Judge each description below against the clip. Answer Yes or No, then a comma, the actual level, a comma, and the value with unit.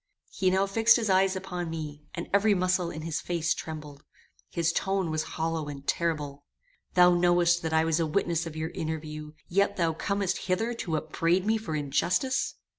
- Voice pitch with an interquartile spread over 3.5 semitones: No, average, 3.1 semitones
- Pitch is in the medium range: Yes, medium, 170 Hz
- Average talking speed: Yes, average, 185 wpm